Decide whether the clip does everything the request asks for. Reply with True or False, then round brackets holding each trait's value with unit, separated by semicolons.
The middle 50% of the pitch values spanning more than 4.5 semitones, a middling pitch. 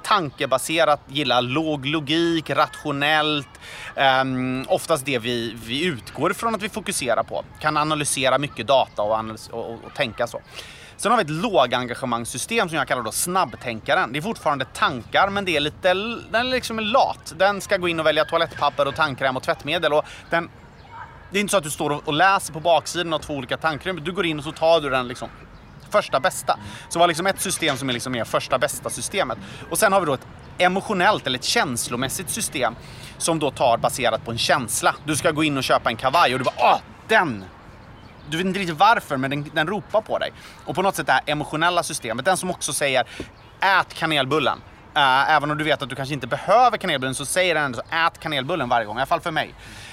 True (5.1 semitones; 150 Hz)